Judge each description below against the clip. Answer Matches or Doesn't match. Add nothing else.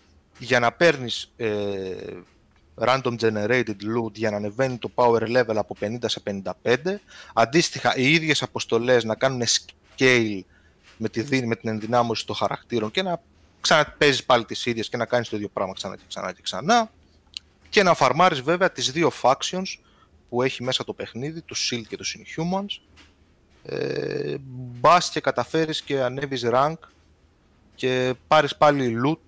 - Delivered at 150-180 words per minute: Matches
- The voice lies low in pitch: Matches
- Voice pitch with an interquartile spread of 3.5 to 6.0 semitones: Matches